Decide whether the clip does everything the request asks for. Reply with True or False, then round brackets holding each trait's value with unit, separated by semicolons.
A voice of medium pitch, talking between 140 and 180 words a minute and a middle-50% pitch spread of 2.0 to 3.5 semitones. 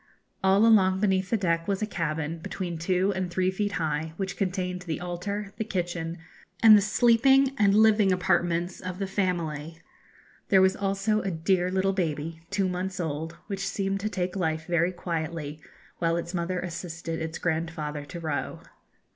True (180 Hz; 170 wpm; 2.9 semitones)